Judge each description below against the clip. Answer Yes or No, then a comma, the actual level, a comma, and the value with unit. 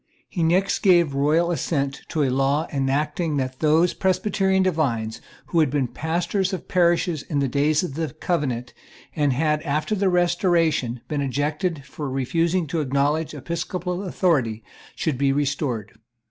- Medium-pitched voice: Yes, medium, 155 Hz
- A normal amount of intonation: Yes, average, 3.9 semitones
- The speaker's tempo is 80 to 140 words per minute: No, average, 155 wpm